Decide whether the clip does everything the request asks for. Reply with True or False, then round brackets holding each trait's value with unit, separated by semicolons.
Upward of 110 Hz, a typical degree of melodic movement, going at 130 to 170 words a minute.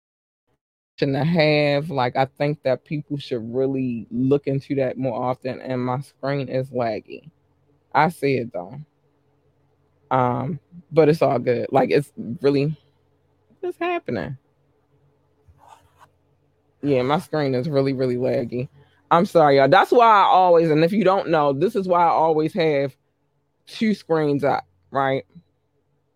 True (140 Hz; 3.4 semitones; 140 wpm)